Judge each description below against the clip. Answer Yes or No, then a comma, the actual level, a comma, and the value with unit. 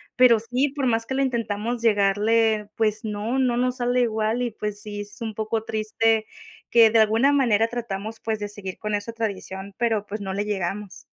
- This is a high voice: Yes, high, 220 Hz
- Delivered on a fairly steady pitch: Yes, narrow, 2.2 semitones